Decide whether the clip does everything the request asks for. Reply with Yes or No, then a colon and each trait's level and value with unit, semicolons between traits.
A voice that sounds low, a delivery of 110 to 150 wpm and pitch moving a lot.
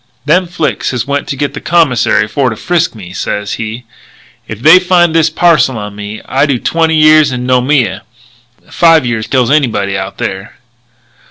No: low, 130 Hz; average, 175 wpm; wide, 6.4 semitones